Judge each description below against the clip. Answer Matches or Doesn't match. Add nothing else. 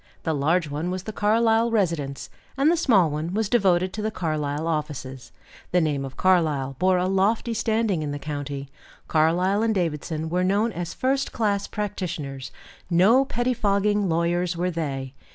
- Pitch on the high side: Doesn't match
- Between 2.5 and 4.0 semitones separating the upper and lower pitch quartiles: Doesn't match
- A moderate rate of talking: Matches